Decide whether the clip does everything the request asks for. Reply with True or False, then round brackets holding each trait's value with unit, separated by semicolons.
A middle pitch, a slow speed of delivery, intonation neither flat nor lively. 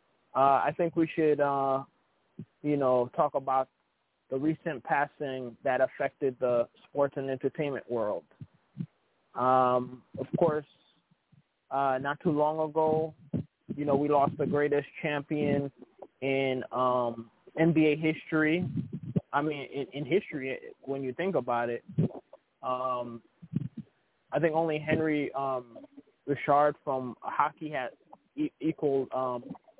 True (145 Hz; 125 wpm; 3.1 semitones)